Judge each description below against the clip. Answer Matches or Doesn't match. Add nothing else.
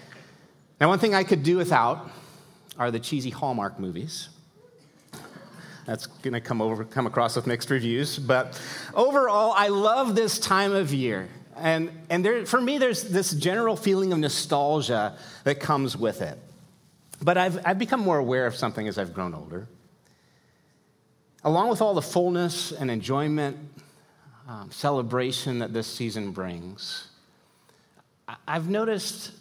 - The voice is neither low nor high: Matches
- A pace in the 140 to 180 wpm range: Matches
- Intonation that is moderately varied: Doesn't match